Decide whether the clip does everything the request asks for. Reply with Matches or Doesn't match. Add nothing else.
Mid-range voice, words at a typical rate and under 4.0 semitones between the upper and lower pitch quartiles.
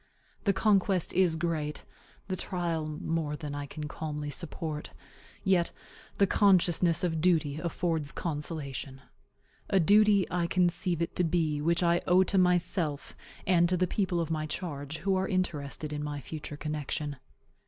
Matches